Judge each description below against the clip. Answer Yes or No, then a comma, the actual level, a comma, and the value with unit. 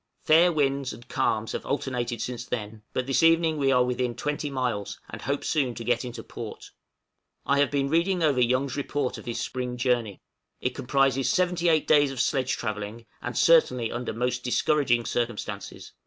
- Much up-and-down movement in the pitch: No, average, 3.1 semitones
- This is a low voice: Yes, low, 130 Hz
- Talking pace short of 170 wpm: No, average, 180 wpm